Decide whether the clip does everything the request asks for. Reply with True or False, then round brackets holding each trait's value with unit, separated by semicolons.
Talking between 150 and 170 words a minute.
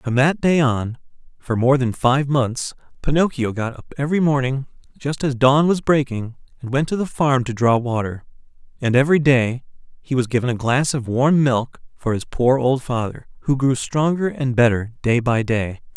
False (190 wpm)